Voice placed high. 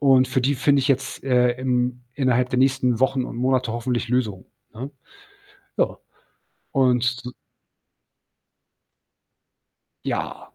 No: low, 125 Hz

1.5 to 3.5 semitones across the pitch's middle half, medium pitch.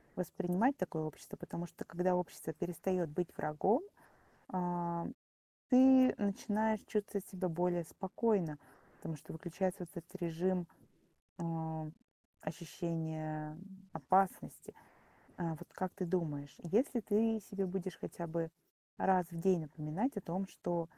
Yes: average, 2.9 semitones; medium, 175 Hz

